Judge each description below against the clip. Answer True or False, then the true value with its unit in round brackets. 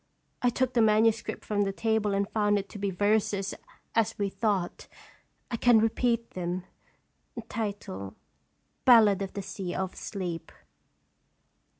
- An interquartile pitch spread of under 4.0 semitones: True (2.4 semitones)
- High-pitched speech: True (205 Hz)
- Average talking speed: False (130 wpm)